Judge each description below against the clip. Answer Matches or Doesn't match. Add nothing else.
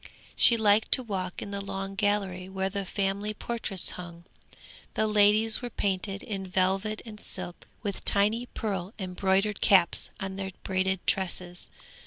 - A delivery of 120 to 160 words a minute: Matches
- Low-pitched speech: Doesn't match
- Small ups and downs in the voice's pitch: Matches